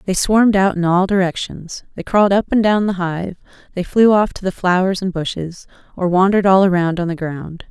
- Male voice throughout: No, female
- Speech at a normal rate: No, fast, 220 wpm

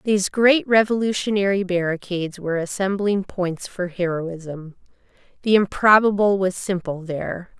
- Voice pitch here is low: No, high, 190 Hz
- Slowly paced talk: Yes, slow, 110 wpm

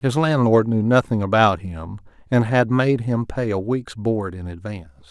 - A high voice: No, low, 110 Hz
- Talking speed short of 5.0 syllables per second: Yes, 4.6 syllables/s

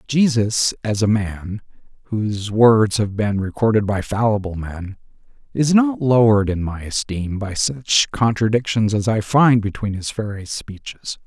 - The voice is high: No, low, 110 Hz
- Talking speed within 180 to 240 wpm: No, average, 150 wpm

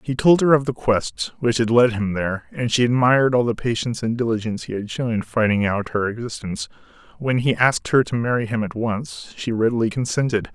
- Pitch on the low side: Yes, low, 115 Hz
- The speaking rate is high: Yes, fast, 220 wpm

